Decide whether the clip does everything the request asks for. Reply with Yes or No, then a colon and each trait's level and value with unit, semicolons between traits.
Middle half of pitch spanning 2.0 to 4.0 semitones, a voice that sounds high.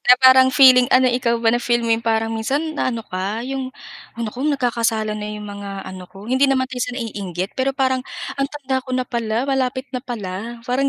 Yes: average, 2.9 semitones; high, 245 Hz